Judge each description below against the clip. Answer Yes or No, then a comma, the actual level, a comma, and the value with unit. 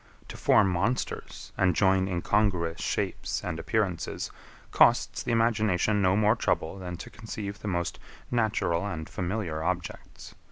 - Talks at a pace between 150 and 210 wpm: No, slow, 135 wpm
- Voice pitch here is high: No, very low, 95 Hz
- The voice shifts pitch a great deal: No, average, 3.6 semitones